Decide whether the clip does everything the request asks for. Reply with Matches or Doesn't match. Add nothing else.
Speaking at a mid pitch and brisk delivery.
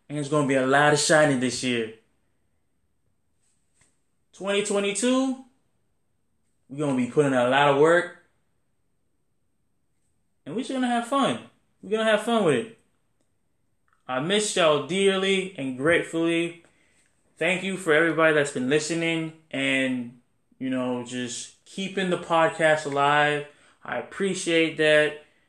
Doesn't match